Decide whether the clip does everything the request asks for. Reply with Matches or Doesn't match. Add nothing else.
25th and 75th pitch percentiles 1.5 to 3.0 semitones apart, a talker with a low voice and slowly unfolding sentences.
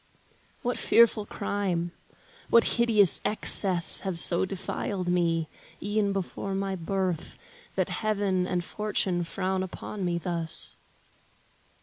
Doesn't match